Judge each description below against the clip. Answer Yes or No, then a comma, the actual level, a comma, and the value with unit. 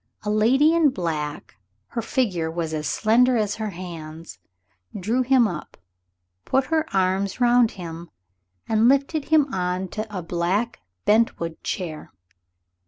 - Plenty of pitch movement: Yes, wide, 6.2 semitones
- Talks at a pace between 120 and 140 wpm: Yes, slow, 135 wpm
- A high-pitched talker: Yes, high, 210 Hz